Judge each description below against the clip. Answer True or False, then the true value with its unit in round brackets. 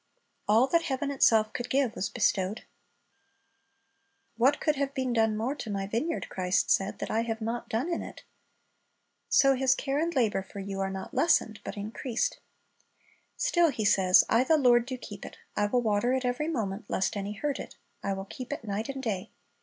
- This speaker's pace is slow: False (195 wpm)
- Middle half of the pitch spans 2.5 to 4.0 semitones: False (4.7 semitones)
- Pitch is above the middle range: True (230 Hz)